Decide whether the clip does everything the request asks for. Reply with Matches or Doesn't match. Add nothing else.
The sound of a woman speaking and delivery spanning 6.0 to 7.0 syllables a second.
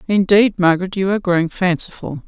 Matches